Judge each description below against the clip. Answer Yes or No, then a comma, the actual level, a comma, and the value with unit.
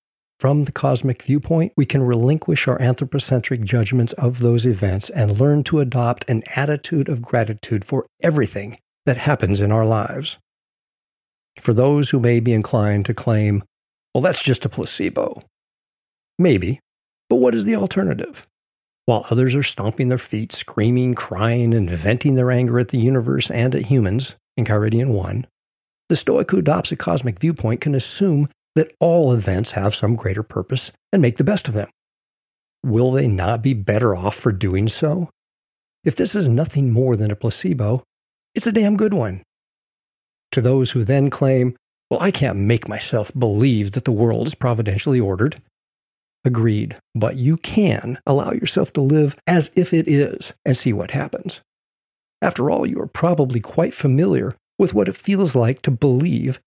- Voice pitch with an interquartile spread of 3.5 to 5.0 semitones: Yes, average, 4.1 semitones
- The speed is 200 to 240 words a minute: No, average, 170 wpm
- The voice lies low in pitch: Yes, low, 125 Hz